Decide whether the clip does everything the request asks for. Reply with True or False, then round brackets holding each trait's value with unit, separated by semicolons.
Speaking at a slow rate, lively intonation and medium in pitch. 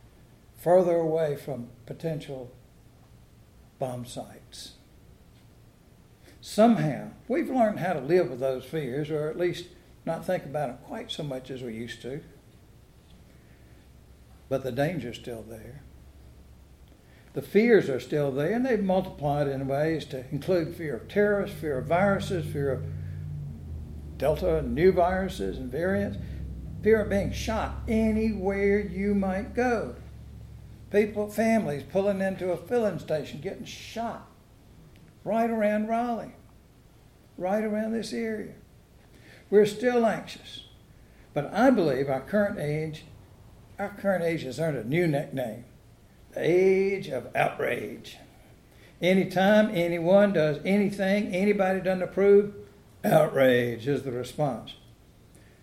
True (125 wpm; 8.4 semitones; 155 Hz)